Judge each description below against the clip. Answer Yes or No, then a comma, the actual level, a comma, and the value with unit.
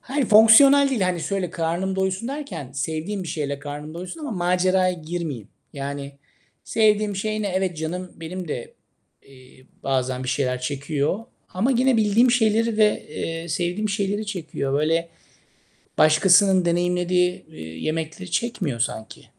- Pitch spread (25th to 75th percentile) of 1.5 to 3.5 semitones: No, average, 5.3 semitones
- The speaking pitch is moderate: Yes, medium, 180 Hz